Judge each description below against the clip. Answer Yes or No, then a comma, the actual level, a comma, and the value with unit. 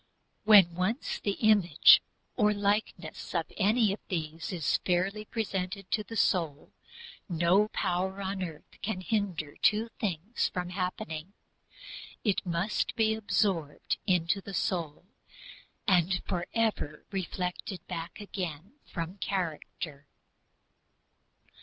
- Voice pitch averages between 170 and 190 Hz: Yes, medium, 185 Hz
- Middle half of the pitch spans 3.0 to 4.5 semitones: Yes, average, 3.4 semitones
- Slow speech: Yes, slow, 110 wpm